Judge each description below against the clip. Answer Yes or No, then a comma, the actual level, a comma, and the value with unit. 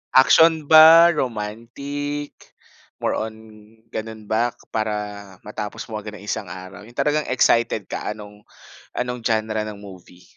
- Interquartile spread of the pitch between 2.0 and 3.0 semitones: No, average, 4.2 semitones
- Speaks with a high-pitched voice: No, low, 110 Hz